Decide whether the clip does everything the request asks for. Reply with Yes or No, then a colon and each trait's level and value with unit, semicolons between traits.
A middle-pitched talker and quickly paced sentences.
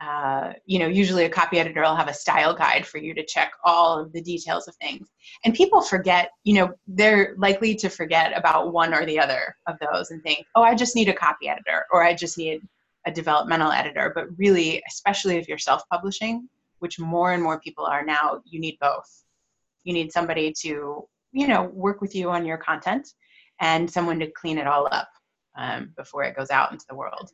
Yes: medium, 170 Hz; fast, 215 wpm